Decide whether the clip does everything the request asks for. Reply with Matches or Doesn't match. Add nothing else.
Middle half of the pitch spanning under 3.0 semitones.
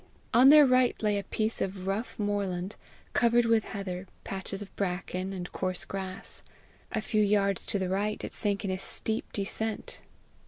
Matches